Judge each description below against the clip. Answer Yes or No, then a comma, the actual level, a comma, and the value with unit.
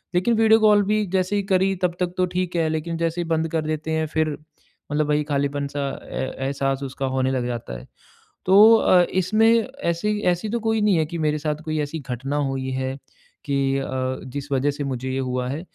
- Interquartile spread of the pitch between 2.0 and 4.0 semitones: No, average, 5.1 semitones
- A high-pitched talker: No, medium, 155 Hz